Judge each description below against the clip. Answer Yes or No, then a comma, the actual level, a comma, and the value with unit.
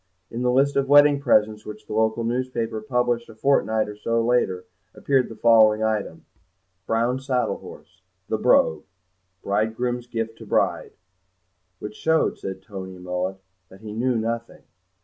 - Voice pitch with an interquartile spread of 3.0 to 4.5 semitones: No, narrow, 2.5 semitones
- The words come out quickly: No, average, 150 wpm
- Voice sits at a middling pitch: No, low, 115 Hz